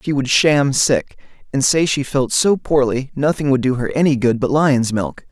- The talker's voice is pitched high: No, low, 135 Hz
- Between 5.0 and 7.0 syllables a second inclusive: No, 4.6 syllables/s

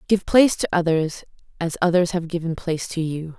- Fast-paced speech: No, average, 195 wpm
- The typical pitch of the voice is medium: Yes, medium, 170 Hz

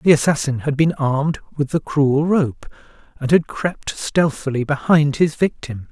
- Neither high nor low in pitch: Yes, medium, 145 Hz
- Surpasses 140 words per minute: Yes, average, 160 wpm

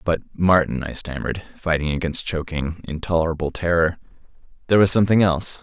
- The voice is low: Yes, very low, 85 Hz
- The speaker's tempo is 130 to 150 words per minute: Yes, average, 140 wpm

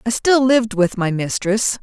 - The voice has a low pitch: No, high, 215 Hz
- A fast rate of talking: No, average, 195 wpm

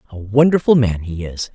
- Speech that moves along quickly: No, average, 195 wpm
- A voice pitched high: No, low, 115 Hz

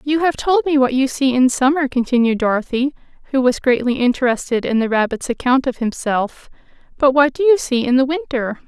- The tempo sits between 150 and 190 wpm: No, average, 200 wpm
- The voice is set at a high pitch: Yes, very high, 265 Hz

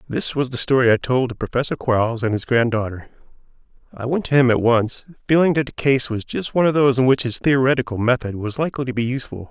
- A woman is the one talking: No, male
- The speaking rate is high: Yes, fast, 235 wpm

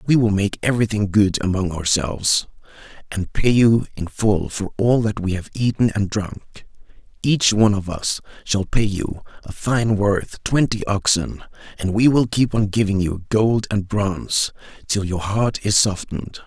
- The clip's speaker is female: No, male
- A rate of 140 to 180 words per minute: Yes, average, 170 wpm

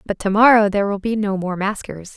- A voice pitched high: Yes, high, 200 Hz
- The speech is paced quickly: Yes, fast, 250 wpm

